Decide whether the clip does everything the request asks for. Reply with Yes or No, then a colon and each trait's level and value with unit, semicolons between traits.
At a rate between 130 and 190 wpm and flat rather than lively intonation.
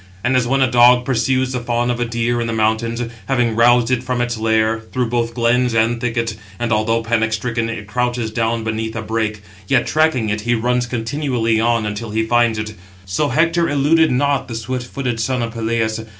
No: fast, 205 wpm; narrow, 1.8 semitones